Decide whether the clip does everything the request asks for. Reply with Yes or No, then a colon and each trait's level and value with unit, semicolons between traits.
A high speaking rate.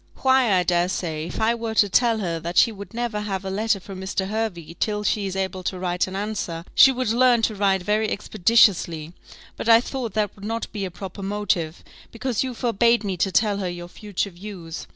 Yes: fast, 220 wpm